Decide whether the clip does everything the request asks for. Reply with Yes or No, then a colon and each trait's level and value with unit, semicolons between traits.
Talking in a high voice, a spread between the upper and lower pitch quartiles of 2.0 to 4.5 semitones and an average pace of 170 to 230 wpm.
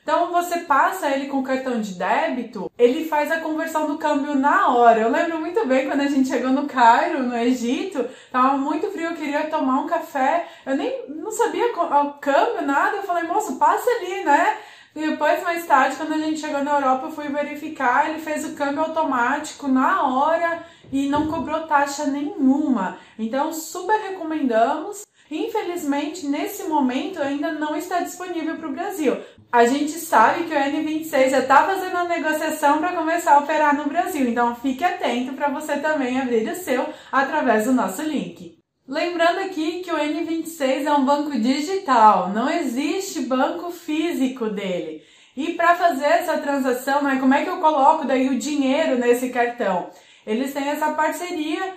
Yes: very high, 295 Hz; average, 3.6 semitones; average, 175 wpm